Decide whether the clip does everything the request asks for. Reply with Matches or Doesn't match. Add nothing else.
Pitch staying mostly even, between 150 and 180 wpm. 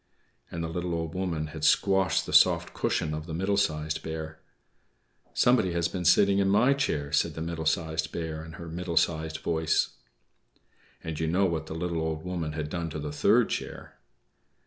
Doesn't match